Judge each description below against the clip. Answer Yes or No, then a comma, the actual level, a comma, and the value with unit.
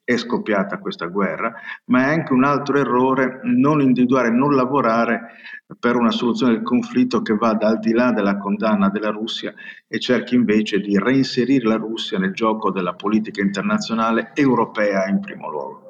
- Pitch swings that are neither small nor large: Yes, average, 3.4 semitones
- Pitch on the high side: No, low, 115 Hz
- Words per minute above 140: Yes, average, 165 wpm